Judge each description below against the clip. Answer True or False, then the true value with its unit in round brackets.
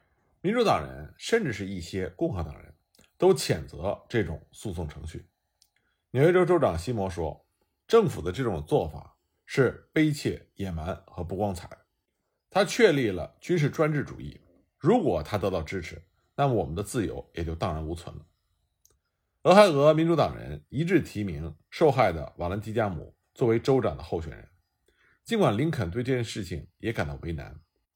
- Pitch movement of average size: False (7.4 semitones)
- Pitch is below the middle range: True (95 Hz)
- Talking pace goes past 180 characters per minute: True (255 characters per minute)